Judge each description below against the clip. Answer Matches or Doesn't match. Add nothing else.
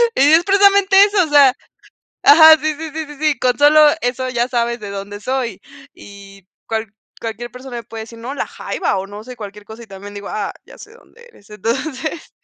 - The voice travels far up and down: Matches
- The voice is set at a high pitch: Matches